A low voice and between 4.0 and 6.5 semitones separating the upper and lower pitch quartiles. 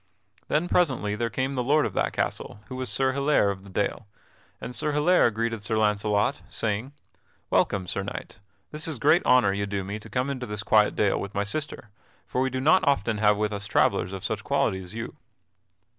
Yes: low, 110 Hz; average, 4.7 semitones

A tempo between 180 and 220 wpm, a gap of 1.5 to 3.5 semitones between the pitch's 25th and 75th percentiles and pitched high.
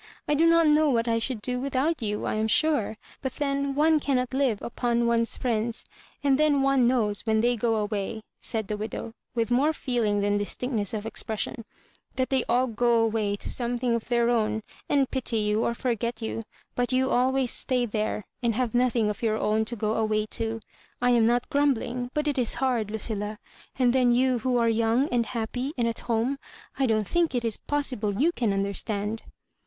Yes: average, 200 wpm; average, 2.9 semitones; high, 235 Hz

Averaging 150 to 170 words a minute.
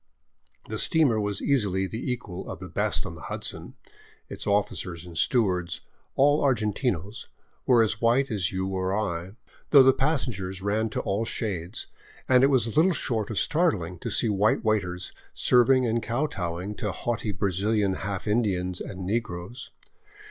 Yes: average, 160 wpm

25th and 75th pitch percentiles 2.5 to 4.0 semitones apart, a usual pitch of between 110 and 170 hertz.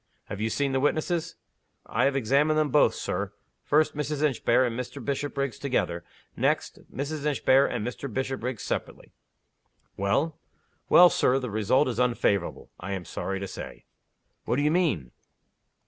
No: average, 4.8 semitones; low, 135 Hz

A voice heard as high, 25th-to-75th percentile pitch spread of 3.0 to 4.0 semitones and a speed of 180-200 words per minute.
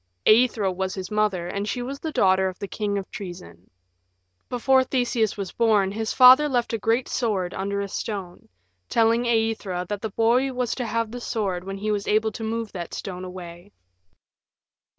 Yes: high, 210 Hz; average, 3.5 semitones; average, 185 wpm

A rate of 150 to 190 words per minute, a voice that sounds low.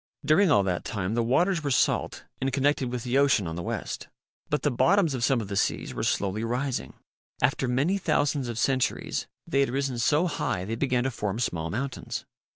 No: fast, 205 wpm; low, 130 Hz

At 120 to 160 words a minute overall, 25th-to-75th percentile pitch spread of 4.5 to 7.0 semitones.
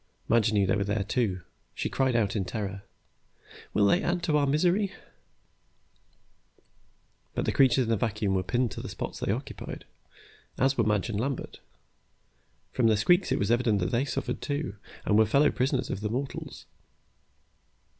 No: average, 170 wpm; average, 4.8 semitones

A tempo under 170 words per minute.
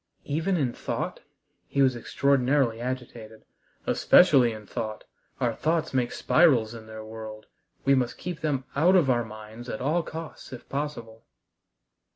Yes: average, 150 wpm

